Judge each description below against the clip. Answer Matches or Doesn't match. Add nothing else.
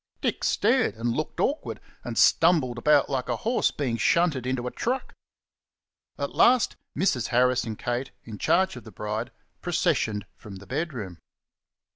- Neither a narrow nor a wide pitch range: Doesn't match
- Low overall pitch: Matches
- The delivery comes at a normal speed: Matches